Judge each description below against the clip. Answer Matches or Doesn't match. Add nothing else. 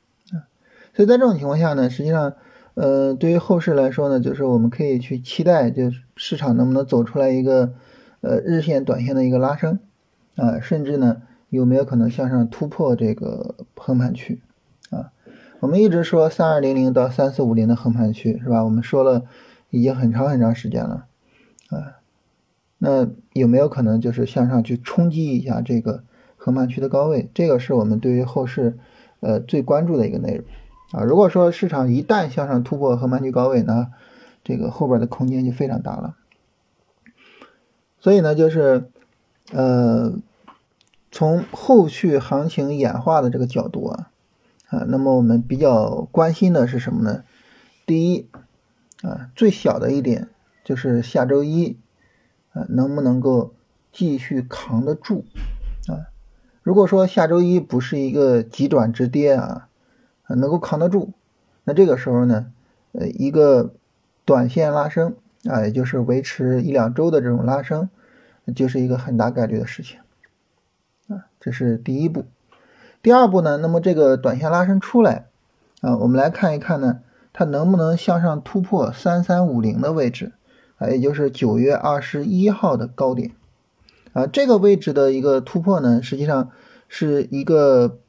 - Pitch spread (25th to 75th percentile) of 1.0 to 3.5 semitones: Doesn't match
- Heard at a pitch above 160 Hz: Doesn't match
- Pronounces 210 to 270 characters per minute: Matches